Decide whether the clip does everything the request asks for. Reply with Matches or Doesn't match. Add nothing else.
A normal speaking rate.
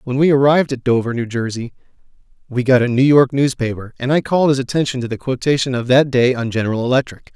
Doesn't match